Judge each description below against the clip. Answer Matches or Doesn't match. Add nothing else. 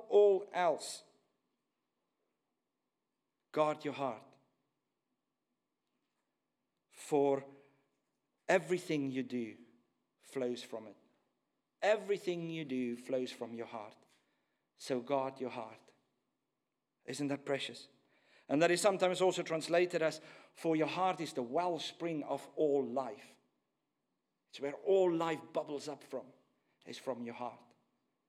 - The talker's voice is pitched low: Doesn't match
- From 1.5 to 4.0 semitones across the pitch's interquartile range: Doesn't match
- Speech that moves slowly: Matches